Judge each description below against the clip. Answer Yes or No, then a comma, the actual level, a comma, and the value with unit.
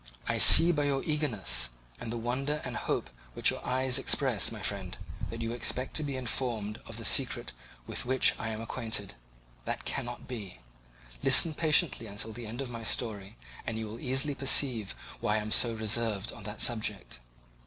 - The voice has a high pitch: No, low, 115 Hz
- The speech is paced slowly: No, average, 180 wpm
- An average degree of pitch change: Yes, average, 3.5 semitones